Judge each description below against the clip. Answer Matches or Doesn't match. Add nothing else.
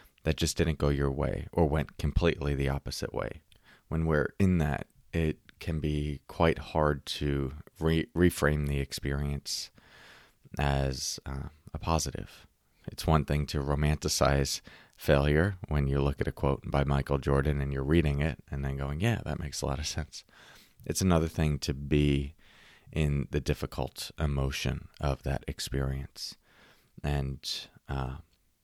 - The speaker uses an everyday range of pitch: Doesn't match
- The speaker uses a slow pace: Doesn't match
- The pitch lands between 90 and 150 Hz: Doesn't match